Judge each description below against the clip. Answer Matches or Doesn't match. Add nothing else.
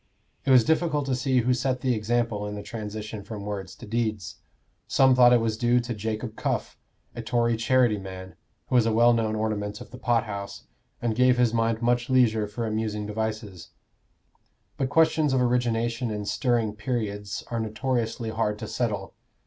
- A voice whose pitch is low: Matches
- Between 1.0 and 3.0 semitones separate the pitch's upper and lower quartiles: Matches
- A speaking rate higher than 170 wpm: Matches